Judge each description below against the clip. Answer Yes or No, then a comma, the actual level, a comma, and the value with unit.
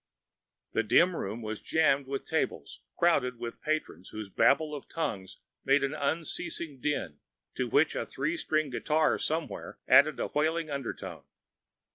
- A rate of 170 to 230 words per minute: No, average, 145 wpm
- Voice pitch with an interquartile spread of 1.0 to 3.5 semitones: No, average, 4.7 semitones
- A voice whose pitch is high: No, medium, 145 Hz